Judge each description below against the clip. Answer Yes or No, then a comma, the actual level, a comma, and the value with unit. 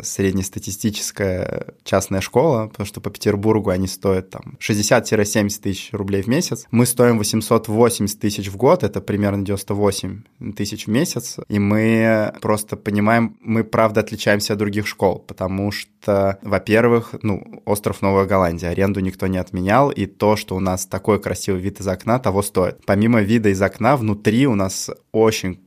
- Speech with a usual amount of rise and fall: No, narrow, 2.1 semitones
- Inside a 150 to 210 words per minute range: Yes, fast, 160 wpm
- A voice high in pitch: No, low, 105 Hz